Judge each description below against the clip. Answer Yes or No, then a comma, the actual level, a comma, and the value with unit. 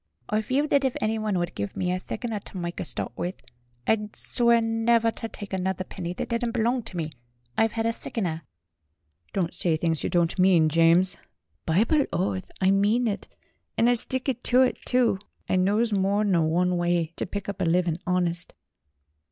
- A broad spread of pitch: No, average, 4.6 semitones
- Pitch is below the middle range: No, high, 195 Hz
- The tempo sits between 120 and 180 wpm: No, average, 195 wpm